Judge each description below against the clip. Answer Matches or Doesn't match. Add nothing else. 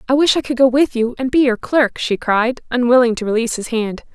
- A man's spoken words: Doesn't match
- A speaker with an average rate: Doesn't match